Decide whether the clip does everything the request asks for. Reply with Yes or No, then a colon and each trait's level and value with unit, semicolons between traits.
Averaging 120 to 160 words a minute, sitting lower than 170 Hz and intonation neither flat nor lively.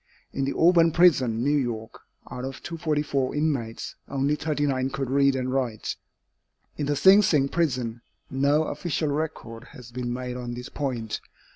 Yes: average, 155 wpm; low, 135 Hz; average, 3.2 semitones